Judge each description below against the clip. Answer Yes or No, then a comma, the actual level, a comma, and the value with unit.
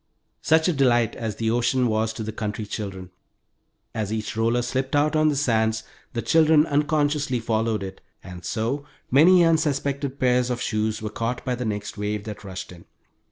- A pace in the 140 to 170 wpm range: No, average, 180 wpm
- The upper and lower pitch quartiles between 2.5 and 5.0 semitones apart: Yes, average, 4.6 semitones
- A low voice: Yes, low, 115 Hz